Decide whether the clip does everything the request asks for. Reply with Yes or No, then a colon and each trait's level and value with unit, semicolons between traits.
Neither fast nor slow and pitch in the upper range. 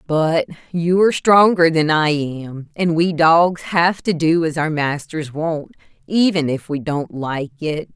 No: average, 175 wpm; medium, 160 Hz